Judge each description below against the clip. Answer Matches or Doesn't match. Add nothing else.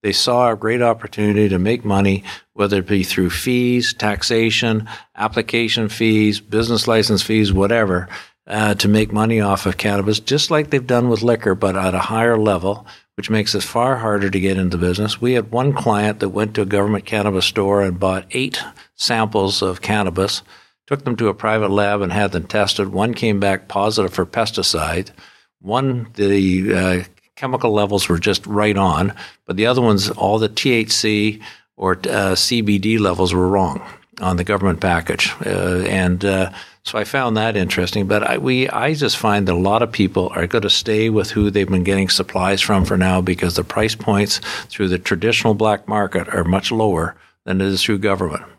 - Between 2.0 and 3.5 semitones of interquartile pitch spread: Matches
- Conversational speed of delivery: Matches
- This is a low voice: Matches